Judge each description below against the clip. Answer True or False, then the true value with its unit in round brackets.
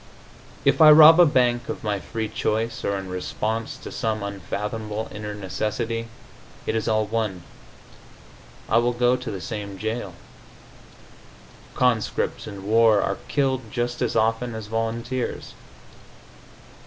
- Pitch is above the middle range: False (110 Hz)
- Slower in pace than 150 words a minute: True (135 wpm)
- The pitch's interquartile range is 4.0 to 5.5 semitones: False (2.4 semitones)